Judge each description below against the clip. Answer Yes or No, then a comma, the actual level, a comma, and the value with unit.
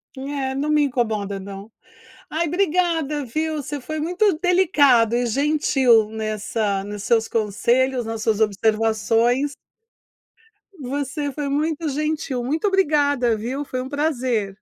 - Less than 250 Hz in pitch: No, very high, 265 Hz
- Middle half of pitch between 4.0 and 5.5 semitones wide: Yes, average, 5.1 semitones